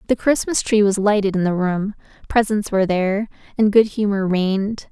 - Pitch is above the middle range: Yes, high, 205 Hz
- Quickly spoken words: No, average, 185 wpm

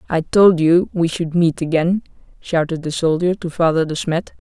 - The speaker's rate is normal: Yes, average, 190 wpm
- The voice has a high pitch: No, medium, 170 Hz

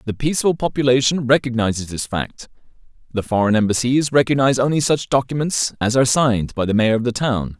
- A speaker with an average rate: Yes, average, 175 wpm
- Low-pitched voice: Yes, low, 125 Hz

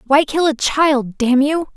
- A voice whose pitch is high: Yes, very high, 280 Hz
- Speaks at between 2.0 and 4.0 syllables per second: Yes, 3.9 syllables/s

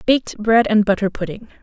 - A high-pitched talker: Yes, high, 210 Hz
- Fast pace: No, average, 185 wpm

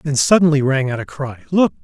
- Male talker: Yes, male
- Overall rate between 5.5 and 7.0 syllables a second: Yes, 5.7 syllables/s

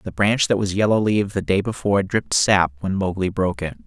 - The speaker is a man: Yes, male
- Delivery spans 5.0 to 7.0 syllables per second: Yes, 6.1 syllables/s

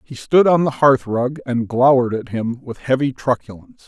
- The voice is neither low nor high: No, low, 130 Hz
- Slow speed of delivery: No, average, 200 wpm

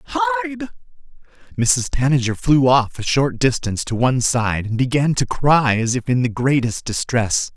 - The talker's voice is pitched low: Yes, low, 125 Hz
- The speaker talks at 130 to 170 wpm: Yes, average, 165 wpm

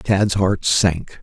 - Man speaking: Yes, male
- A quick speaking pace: No, average, 145 wpm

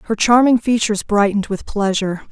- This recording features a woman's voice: Yes, female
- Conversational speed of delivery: Yes, average, 155 wpm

